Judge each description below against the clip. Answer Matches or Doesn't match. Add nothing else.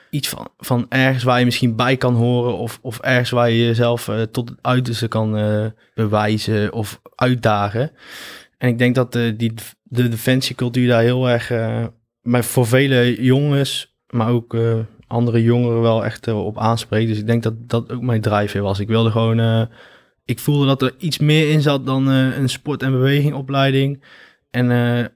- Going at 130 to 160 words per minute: Doesn't match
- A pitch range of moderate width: Doesn't match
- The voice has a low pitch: Matches